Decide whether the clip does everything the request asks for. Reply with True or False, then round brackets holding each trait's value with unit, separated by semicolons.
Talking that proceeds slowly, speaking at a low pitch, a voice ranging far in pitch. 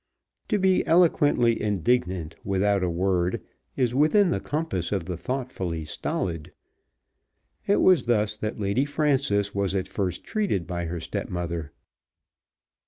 True (130 wpm; 100 Hz; 7.4 semitones)